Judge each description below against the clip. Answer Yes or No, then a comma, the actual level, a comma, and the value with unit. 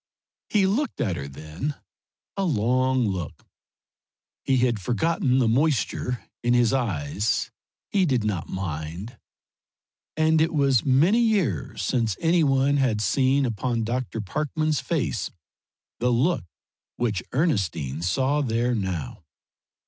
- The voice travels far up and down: Yes, wide, 6.1 semitones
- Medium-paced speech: No, slow, 125 wpm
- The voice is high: No, low, 125 Hz